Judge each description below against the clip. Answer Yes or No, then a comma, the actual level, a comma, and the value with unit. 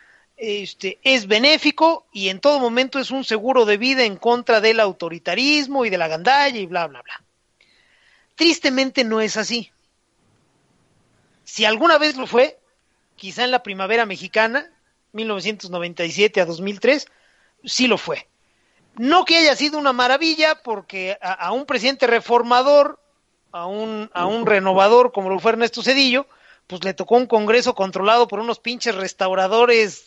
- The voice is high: Yes, high, 230 Hz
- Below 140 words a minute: No, average, 150 wpm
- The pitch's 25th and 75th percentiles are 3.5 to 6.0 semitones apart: Yes, average, 5.2 semitones